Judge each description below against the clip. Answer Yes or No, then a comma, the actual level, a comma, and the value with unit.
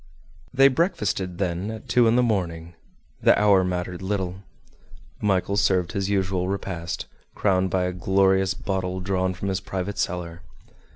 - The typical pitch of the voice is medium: No, very low, 95 Hz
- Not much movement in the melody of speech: Yes, narrow, 1.6 semitones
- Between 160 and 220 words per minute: No, average, 150 wpm